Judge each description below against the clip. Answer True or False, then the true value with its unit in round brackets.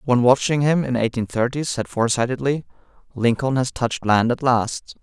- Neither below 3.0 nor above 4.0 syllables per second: False (5.4 syllables/s)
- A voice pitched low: True (125 Hz)